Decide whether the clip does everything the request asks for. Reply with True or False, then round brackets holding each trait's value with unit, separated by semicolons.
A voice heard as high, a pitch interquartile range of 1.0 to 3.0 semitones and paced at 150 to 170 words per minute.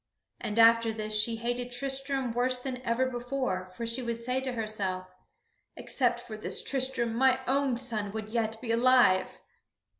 True (240 Hz; 2.5 semitones; 160 wpm)